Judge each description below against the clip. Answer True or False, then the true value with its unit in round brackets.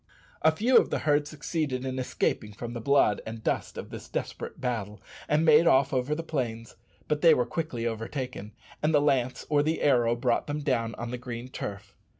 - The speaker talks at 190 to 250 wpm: True (200 wpm)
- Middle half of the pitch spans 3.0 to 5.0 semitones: True (4.3 semitones)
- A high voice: False (130 Hz)